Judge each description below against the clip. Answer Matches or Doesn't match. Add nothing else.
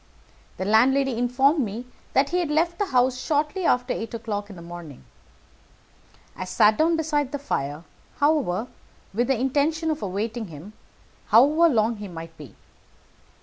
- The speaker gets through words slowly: Doesn't match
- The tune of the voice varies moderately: Doesn't match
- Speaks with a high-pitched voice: Matches